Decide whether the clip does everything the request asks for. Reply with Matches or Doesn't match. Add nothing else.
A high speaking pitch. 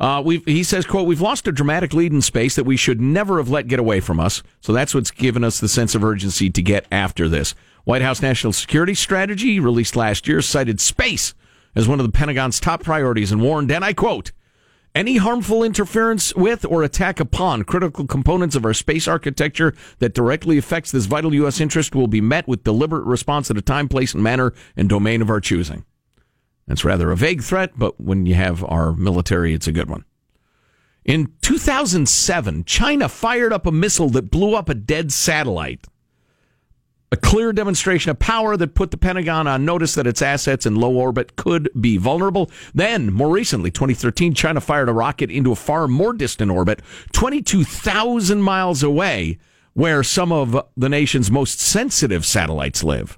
Doesn't match